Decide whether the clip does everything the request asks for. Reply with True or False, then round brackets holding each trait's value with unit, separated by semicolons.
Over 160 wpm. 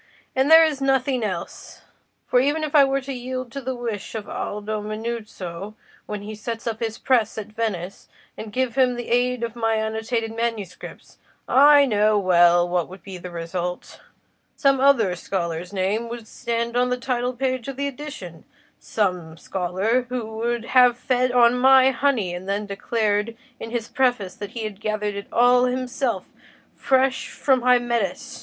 True (170 wpm)